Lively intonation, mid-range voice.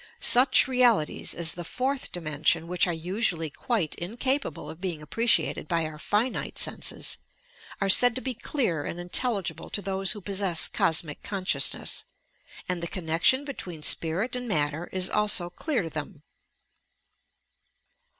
Yes: wide, 6.0 semitones; medium, 180 Hz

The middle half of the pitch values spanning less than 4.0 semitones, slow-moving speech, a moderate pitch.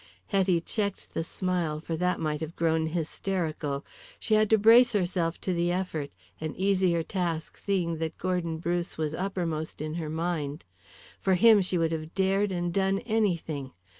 No: average, 3.1 semitones; average, 165 wpm; medium, 175 Hz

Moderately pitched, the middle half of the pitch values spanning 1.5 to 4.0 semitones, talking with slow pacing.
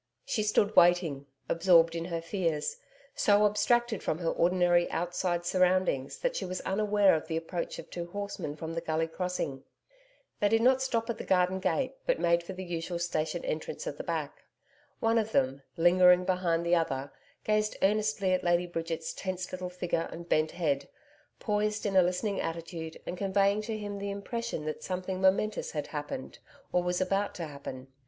No: medium, 180 Hz; average, 3.6 semitones; average, 180 wpm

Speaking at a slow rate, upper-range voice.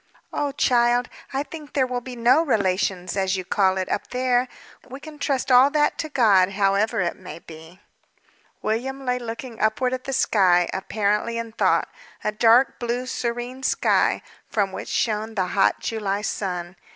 No: average, 170 wpm; high, 230 Hz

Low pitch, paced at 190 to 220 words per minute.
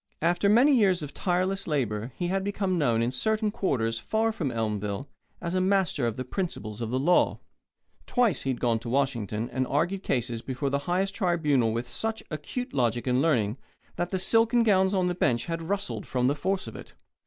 No: medium, 155 Hz; average, 200 wpm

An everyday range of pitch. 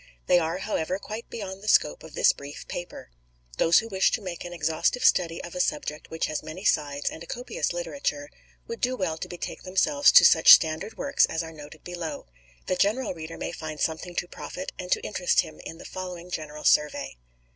Yes: average, 4.2 semitones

